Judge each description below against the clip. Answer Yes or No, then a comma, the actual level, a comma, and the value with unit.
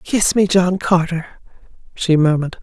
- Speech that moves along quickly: No, slow, 135 wpm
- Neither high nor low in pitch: Yes, medium, 175 Hz